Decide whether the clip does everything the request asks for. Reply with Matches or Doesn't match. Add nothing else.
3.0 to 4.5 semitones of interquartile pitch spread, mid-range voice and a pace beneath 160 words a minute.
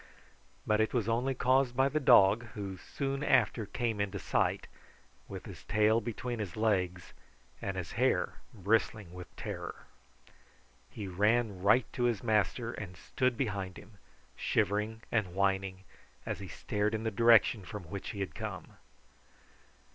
Doesn't match